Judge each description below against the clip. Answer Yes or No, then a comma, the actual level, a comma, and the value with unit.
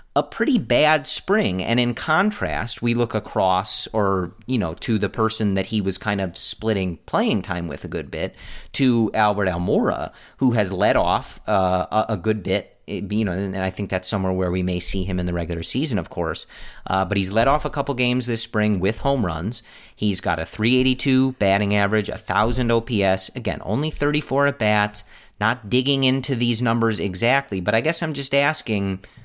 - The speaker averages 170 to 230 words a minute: Yes, average, 195 wpm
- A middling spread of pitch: Yes, average, 4.2 semitones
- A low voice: Yes, low, 105 Hz